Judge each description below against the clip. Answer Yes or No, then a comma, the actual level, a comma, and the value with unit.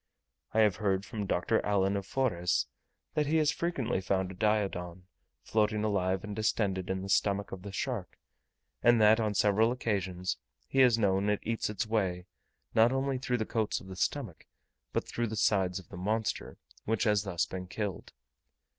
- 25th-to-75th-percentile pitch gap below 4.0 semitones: Yes, average, 3.0 semitones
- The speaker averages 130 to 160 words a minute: No, average, 180 wpm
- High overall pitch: No, low, 105 Hz